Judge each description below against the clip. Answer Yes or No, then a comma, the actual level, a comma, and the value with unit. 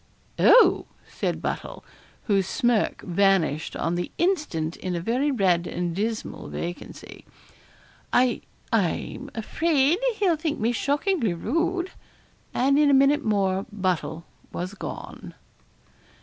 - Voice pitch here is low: No, high, 225 Hz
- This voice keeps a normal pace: No, slow, 120 wpm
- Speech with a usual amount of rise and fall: No, wide, 8.1 semitones